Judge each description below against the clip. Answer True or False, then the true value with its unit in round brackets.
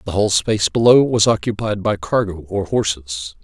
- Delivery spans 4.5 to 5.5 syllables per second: True (5.2 syllables/s)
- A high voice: False (100 Hz)